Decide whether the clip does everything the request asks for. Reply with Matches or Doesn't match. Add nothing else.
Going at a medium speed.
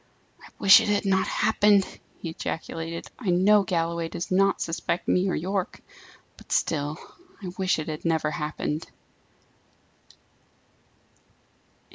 Doesn't match